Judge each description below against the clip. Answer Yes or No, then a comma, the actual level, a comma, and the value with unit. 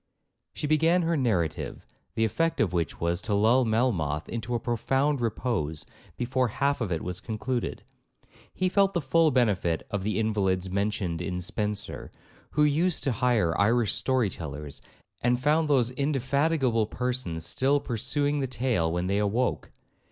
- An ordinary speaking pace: Yes, average, 155 wpm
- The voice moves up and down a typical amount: No, wide, 5.8 semitones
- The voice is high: No, low, 120 Hz